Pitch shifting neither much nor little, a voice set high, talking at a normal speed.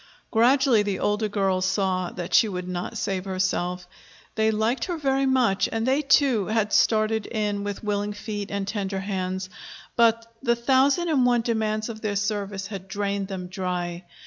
Yes: average, 3.2 semitones; high, 205 Hz; average, 170 wpm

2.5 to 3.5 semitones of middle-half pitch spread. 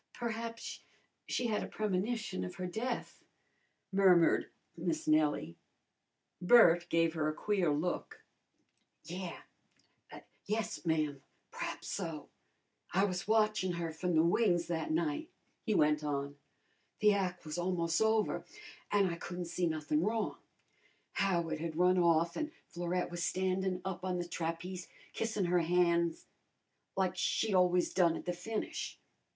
Yes: average, 2.8 semitones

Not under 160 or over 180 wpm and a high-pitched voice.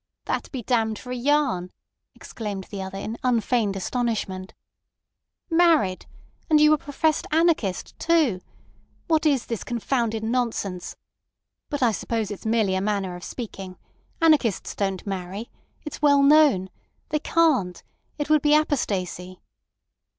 No: slow, 135 wpm; high, 230 Hz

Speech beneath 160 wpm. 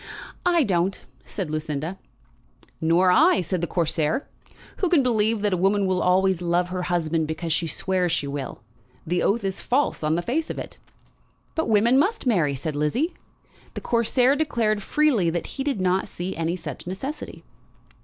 No: average, 175 wpm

